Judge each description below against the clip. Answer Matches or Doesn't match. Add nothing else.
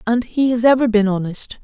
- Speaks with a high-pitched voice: Matches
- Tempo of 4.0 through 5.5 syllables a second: Matches